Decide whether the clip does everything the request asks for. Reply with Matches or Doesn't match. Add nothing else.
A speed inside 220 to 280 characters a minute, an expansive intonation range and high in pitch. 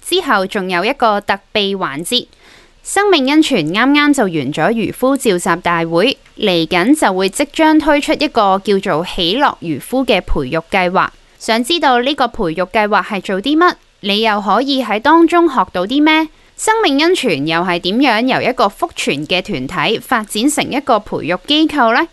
Matches